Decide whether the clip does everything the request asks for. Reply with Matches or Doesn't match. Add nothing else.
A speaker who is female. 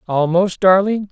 Matches